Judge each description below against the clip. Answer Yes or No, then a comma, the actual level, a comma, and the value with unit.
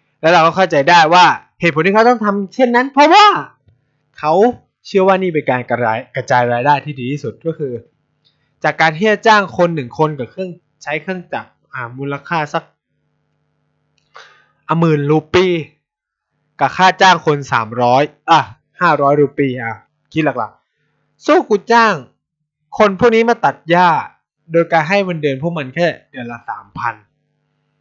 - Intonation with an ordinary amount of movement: Yes, average, 4.5 semitones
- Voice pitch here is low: No, medium, 155 Hz